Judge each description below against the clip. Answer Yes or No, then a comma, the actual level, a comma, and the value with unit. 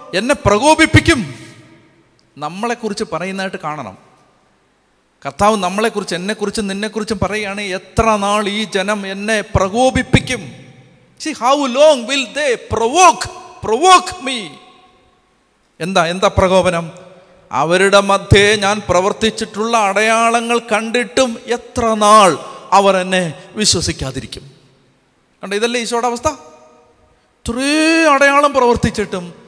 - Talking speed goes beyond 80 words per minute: No, average, 75 wpm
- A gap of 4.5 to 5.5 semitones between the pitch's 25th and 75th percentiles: No, average, 4.1 semitones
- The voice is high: Yes, high, 215 Hz